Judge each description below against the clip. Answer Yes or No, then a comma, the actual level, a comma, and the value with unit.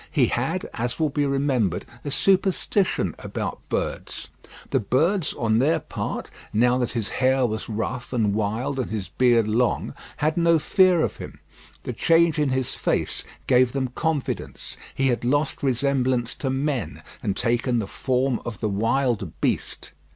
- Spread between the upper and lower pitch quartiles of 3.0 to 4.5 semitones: Yes, average, 3.8 semitones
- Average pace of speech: Yes, average, 160 wpm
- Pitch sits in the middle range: No, low, 130 Hz